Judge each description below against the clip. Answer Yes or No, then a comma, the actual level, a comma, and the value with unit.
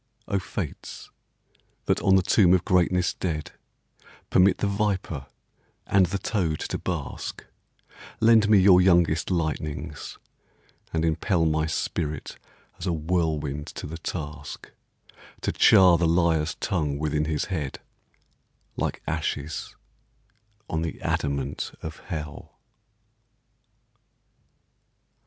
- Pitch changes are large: No, average, 3.1 semitones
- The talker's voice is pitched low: Yes, very low, 80 Hz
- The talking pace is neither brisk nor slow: No, slow, 115 wpm